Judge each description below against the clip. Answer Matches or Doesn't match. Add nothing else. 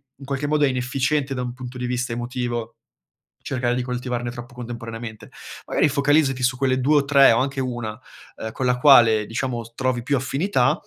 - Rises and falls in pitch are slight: Matches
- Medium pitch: Doesn't match